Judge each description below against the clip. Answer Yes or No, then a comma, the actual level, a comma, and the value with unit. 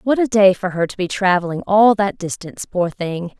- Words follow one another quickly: Yes, fast, 230 wpm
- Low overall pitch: No, high, 195 Hz